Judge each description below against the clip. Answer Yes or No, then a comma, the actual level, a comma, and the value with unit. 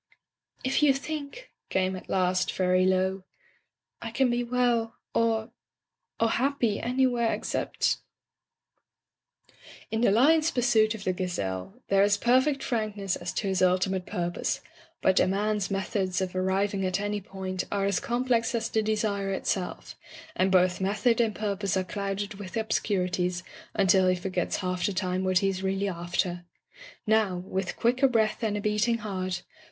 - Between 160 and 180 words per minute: Yes, average, 165 wpm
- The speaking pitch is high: Yes, high, 200 Hz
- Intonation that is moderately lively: Yes, average, 3.5 semitones